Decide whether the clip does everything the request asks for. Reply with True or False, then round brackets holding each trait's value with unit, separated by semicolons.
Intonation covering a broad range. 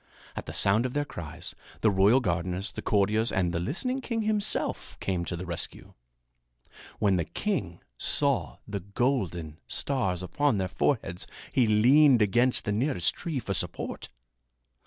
True (6.3 semitones)